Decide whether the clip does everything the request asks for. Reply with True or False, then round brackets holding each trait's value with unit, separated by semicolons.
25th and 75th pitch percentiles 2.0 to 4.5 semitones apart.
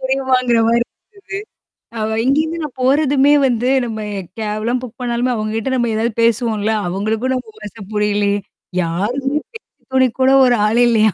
True (3.2 semitones)